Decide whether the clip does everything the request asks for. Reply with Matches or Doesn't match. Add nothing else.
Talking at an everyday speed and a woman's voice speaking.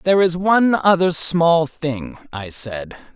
Doesn't match